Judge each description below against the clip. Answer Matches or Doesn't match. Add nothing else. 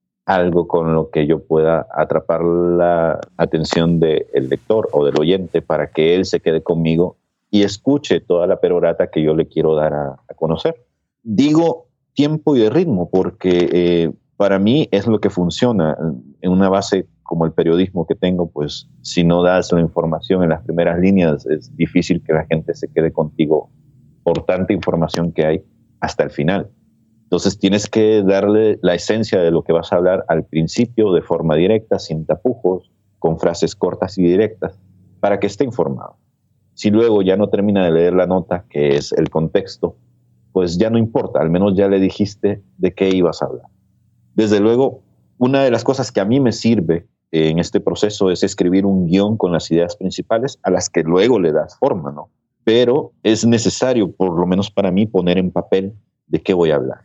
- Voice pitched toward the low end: Matches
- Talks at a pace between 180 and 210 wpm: Matches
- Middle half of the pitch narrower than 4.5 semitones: Matches